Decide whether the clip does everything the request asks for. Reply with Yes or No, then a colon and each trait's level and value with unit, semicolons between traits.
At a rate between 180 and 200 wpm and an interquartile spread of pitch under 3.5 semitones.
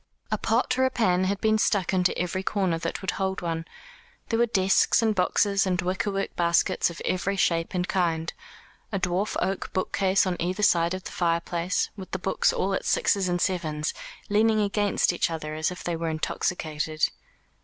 Yes: average, 185 wpm; narrow, 2.6 semitones